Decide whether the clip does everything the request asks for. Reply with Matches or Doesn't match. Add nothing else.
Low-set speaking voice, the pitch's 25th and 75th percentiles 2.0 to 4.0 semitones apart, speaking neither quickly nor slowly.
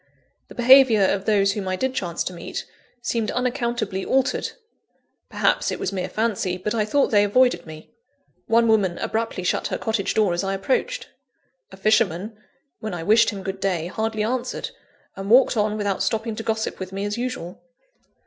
Doesn't match